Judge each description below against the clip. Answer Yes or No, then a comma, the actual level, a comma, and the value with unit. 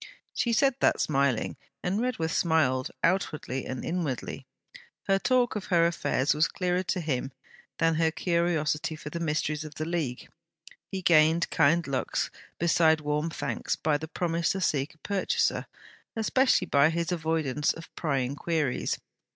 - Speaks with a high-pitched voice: No, medium, 160 Hz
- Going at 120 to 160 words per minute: Yes, average, 150 wpm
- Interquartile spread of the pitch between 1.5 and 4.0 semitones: Yes, average, 2.7 semitones